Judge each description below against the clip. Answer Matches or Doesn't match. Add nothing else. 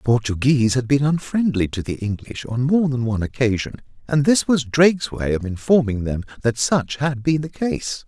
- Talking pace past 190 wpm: Matches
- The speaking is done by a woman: Doesn't match